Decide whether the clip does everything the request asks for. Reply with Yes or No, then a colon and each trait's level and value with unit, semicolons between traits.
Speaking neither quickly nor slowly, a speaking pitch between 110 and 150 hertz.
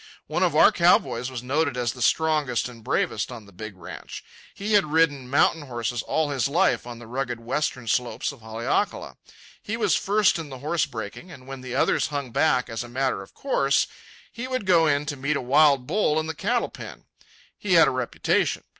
No: fast, 210 wpm; low, 135 Hz